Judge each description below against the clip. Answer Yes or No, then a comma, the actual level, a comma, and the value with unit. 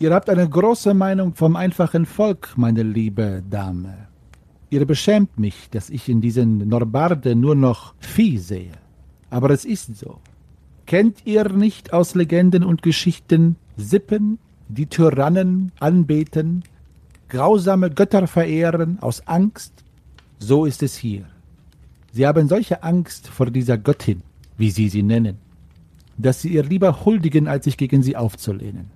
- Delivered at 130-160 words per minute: Yes, average, 140 wpm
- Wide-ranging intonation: Yes, wide, 8.6 semitones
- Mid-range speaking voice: Yes, medium, 145 Hz